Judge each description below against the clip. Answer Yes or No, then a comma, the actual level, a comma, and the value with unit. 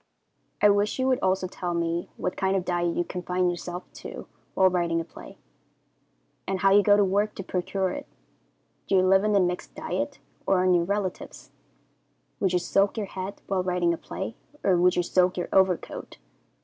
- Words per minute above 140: Yes, average, 195 wpm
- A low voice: No, medium, 185 Hz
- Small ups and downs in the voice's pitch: Yes, narrow, 1.7 semitones